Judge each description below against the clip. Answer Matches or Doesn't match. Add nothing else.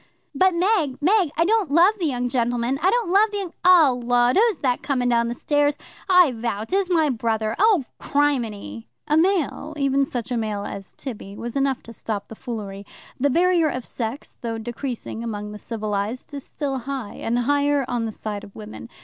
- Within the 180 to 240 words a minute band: Matches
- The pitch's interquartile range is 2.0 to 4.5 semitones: Doesn't match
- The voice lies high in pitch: Matches